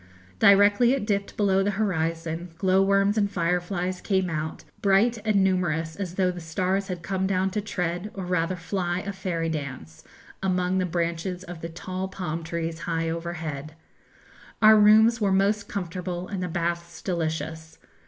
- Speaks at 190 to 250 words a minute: No, average, 160 wpm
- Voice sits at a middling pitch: Yes, medium, 180 Hz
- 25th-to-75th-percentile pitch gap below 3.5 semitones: Yes, average, 2.8 semitones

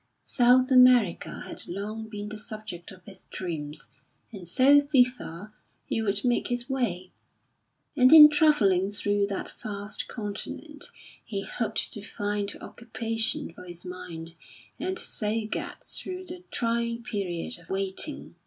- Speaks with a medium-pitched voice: No, high, 215 Hz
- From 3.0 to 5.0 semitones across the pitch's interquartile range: Yes, average, 4.2 semitones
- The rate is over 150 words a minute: No, slow, 135 wpm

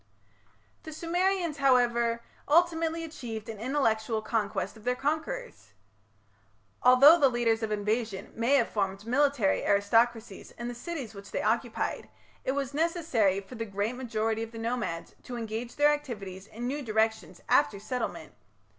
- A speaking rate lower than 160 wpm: Yes, average, 145 wpm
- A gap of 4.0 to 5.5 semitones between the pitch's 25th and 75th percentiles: Yes, average, 4.5 semitones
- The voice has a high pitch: Yes, high, 235 Hz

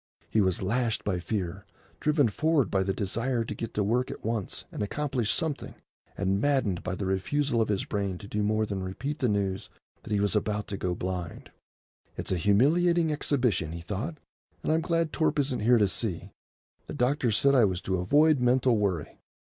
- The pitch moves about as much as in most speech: No, wide, 6.1 semitones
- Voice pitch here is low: Yes, low, 110 Hz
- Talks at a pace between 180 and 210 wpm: Yes, average, 195 wpm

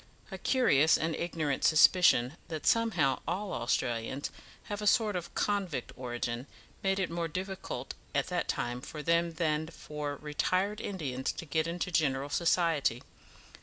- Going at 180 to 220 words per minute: No, average, 145 wpm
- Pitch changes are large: No, average, 4.6 semitones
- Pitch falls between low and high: Yes, medium, 160 Hz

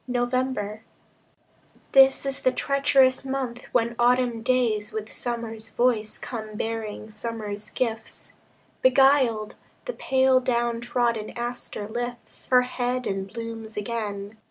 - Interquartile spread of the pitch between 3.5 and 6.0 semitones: No, average, 2.7 semitones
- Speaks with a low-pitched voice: No, high, 235 Hz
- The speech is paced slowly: Yes, slow, 115 wpm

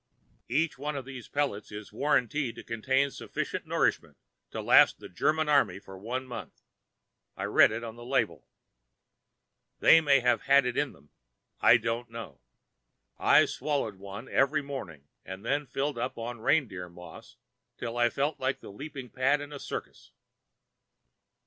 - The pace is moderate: Yes, average, 160 wpm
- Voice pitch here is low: Yes, low, 125 Hz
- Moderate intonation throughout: Yes, average, 3.9 semitones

